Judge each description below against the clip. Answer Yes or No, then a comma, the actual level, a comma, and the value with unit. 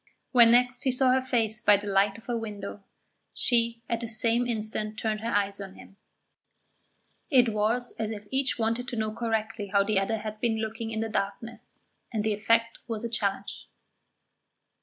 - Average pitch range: No, narrow, 1.9 semitones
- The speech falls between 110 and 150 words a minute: No, average, 185 wpm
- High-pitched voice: Yes, high, 225 Hz